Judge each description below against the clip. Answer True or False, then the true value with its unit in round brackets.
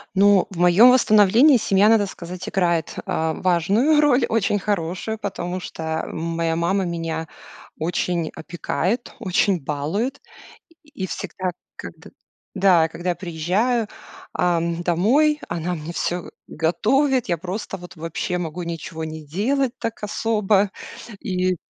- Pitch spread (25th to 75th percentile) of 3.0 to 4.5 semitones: True (4.0 semitones)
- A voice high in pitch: False (180 Hz)